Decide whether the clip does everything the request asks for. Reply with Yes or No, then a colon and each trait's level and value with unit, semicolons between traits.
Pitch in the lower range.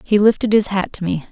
No: high, 200 Hz